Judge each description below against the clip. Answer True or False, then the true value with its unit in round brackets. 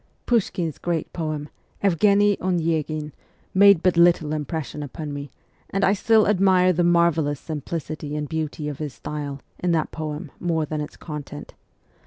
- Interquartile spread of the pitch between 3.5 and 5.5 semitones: False (3.1 semitones)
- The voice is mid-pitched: True (160 Hz)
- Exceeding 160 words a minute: False (155 wpm)